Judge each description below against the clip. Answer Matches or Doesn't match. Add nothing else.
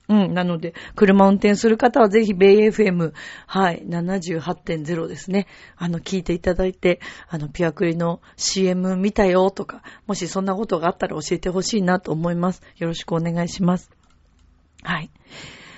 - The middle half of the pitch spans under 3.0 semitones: Matches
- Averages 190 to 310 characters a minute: Matches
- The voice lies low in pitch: Doesn't match